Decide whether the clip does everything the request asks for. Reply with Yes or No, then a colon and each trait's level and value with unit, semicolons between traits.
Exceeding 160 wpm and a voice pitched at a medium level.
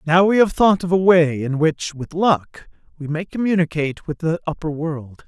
Yes: fast, 205 wpm; medium, 165 Hz